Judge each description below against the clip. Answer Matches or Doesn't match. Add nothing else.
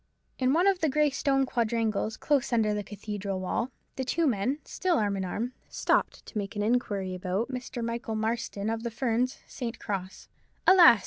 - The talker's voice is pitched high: Matches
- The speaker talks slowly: Doesn't match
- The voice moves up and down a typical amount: Matches